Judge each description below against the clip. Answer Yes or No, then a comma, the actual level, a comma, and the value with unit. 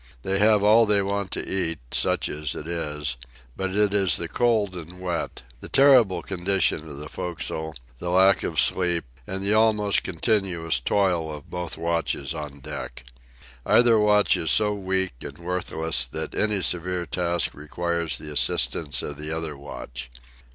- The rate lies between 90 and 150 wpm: No, average, 165 wpm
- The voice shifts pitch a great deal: No, average, 4.0 semitones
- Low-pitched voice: Yes, very low, 90 Hz